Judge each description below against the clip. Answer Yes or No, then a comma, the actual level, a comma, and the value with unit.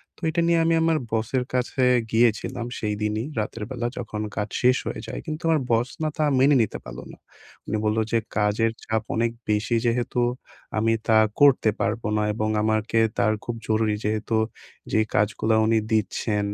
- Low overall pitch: Yes, low, 110 Hz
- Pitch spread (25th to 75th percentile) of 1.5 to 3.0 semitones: Yes, narrow, 2.4 semitones